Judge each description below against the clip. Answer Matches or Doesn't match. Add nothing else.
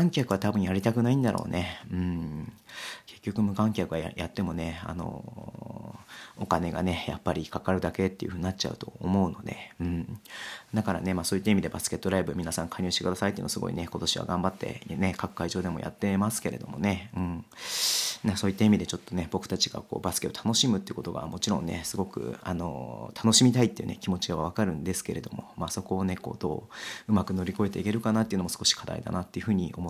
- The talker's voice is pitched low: Matches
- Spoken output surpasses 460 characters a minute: Matches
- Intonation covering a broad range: Doesn't match